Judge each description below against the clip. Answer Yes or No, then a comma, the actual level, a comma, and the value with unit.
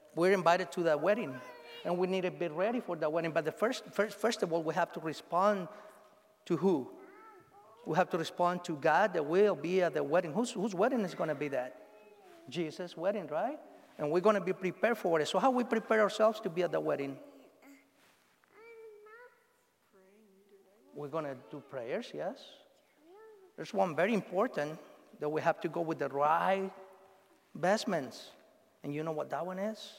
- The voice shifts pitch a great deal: Yes, wide, 5.7 semitones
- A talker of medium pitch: No, high, 195 Hz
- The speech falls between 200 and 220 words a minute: No, average, 190 wpm